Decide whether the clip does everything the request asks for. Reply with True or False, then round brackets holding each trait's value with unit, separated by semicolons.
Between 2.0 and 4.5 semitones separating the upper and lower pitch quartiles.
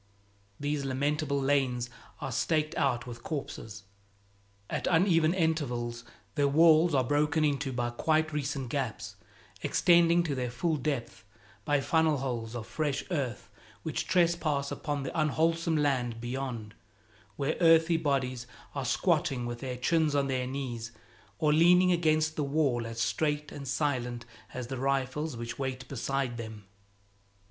True (4.0 semitones)